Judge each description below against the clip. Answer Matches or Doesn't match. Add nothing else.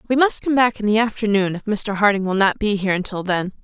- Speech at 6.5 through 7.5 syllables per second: Doesn't match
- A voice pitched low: Doesn't match